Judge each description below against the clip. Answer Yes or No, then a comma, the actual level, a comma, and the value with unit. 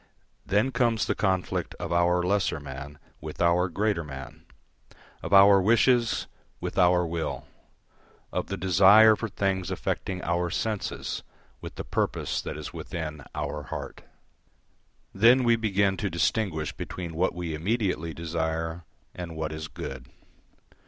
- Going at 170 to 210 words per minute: No, average, 140 wpm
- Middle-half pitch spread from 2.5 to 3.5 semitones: No, average, 3.9 semitones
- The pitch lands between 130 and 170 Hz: No, very low, 90 Hz